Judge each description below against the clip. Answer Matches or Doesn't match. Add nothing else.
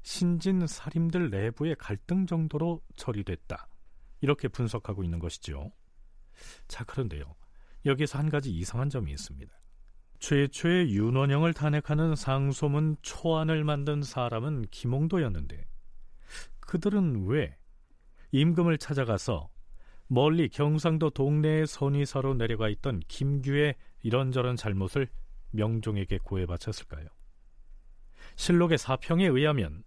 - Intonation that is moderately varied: Doesn't match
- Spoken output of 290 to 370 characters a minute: Doesn't match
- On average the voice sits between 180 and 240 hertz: Doesn't match